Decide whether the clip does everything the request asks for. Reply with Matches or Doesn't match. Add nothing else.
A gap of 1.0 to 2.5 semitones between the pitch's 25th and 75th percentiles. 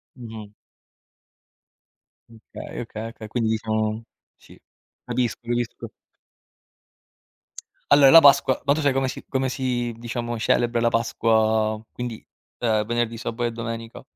Matches